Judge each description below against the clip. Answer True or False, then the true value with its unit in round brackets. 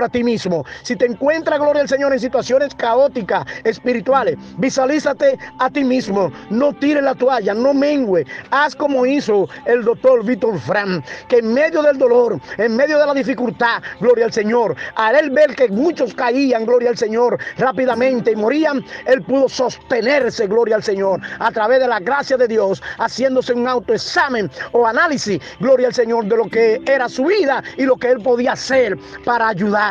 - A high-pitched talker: True (255 Hz)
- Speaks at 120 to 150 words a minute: False (180 wpm)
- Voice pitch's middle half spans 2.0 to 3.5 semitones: True (3.2 semitones)